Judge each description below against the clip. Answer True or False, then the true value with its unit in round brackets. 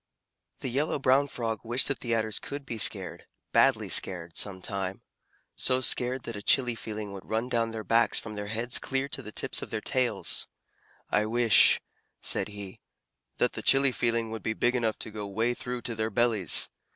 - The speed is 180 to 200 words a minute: True (195 wpm)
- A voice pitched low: True (115 Hz)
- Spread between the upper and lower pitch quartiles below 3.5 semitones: True (2.6 semitones)